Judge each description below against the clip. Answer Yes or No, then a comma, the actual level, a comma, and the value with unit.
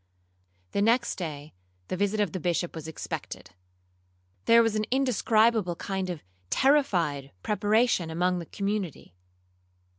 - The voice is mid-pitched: No, high, 195 Hz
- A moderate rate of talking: No, slow, 125 wpm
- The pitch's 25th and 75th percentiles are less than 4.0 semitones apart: No, average, 4.5 semitones